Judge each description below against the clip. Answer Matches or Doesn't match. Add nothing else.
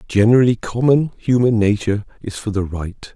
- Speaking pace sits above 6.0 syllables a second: Doesn't match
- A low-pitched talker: Matches